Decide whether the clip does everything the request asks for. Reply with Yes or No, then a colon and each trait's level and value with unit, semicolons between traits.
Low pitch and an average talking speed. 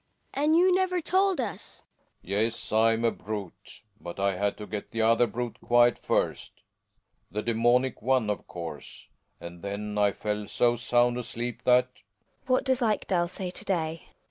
Yes: low, 120 Hz; average, 185 wpm